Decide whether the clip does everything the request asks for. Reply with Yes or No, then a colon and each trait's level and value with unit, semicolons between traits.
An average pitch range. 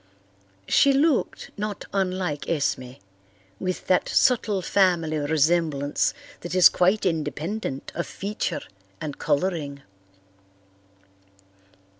Yes: average, 4.6 semitones